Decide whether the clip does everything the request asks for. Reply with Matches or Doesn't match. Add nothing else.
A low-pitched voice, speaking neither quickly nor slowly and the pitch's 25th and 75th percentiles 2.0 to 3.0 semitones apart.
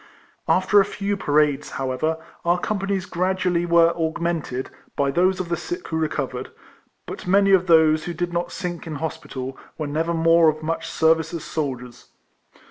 Doesn't match